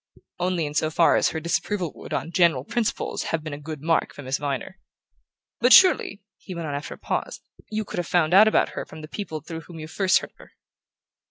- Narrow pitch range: No, average, 3.2 semitones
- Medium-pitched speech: Yes, medium, 165 Hz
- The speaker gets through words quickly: Yes, fast, 235 wpm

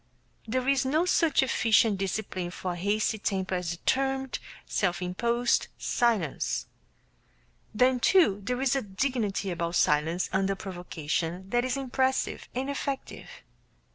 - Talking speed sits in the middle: No, slow, 130 wpm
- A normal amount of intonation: No, wide, 6.1 semitones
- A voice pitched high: Yes, high, 215 Hz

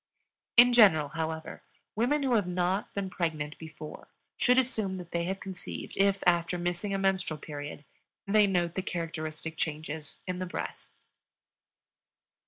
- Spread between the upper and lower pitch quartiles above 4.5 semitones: No, average, 3.6 semitones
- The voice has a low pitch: No, medium, 175 Hz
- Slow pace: No, average, 145 wpm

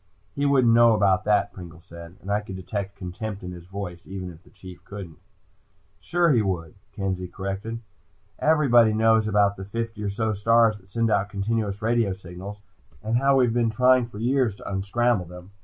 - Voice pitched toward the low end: Yes, low, 105 Hz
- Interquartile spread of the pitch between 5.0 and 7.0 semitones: No, average, 3.4 semitones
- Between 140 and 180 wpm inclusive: No, average, 190 wpm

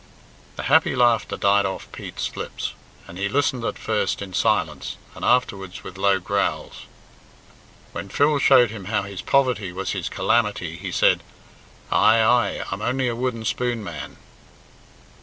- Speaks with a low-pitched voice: Yes, low, 105 Hz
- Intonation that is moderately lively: Yes, average, 4.0 semitones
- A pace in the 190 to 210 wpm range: No, average, 155 wpm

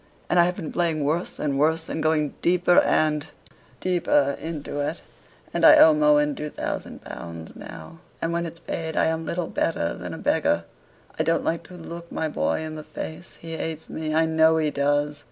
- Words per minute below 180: No, average, 200 wpm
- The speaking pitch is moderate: Yes, medium, 160 Hz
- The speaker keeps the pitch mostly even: Yes, narrow, 1.9 semitones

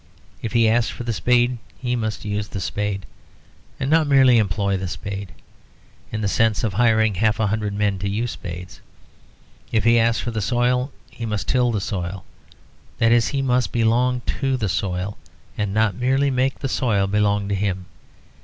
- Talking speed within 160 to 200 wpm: Yes, average, 185 wpm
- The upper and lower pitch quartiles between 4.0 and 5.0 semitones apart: No, average, 3.3 semitones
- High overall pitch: No, low, 110 Hz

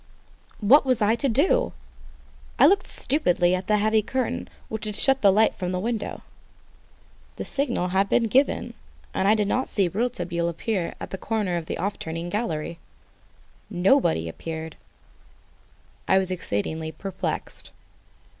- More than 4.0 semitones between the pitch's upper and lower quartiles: Yes, average, 4.7 semitones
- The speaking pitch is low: No, high, 200 Hz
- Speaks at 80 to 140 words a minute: No, average, 150 wpm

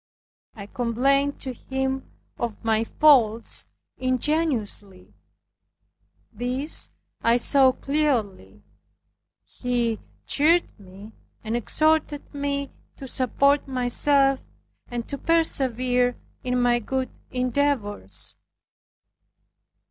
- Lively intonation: No, average, 3.4 semitones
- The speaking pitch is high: Yes, very high, 255 Hz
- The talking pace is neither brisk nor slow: No, slow, 80 wpm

